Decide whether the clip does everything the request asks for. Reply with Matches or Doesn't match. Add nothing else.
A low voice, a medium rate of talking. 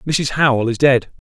Matches